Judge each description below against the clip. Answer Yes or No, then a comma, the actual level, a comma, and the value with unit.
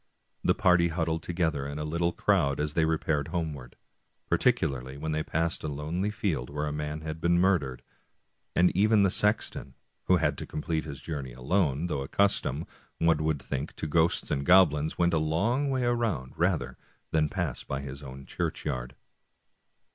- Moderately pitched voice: No, very low, 80 Hz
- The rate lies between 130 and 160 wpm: No, average, 170 wpm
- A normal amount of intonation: Yes, average, 3.5 semitones